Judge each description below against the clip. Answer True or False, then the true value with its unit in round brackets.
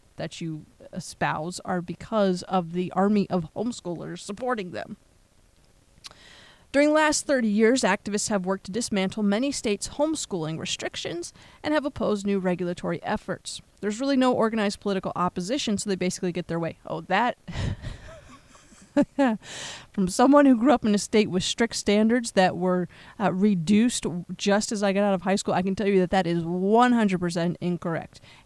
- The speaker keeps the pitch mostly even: False (3.8 semitones)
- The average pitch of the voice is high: True (200 Hz)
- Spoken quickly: False (165 wpm)